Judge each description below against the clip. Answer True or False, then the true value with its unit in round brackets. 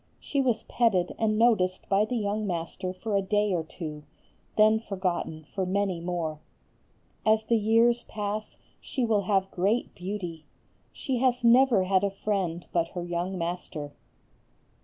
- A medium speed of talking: True (155 wpm)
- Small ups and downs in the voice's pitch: False (3.7 semitones)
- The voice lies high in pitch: True (195 Hz)